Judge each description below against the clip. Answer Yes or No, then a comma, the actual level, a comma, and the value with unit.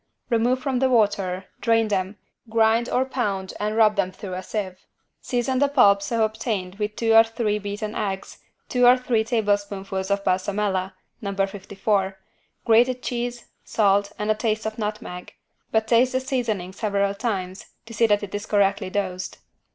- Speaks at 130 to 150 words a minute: No, average, 165 wpm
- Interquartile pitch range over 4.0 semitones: No, average, 2.7 semitones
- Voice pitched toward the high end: Yes, high, 210 Hz